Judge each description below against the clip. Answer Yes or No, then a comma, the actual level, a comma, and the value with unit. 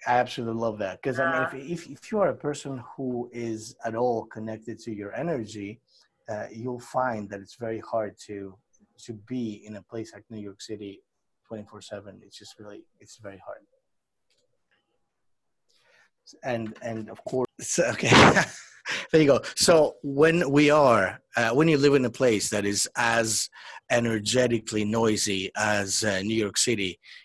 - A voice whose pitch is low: Yes, low, 115 Hz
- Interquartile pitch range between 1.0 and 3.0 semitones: No, average, 3.4 semitones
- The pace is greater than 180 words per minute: No, average, 165 wpm